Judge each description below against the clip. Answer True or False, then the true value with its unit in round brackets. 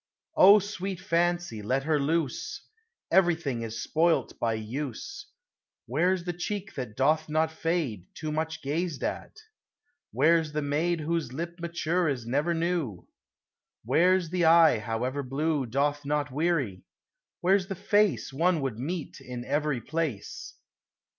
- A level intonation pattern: False (4.3 semitones)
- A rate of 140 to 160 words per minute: True (145 wpm)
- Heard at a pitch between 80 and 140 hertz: False (155 Hz)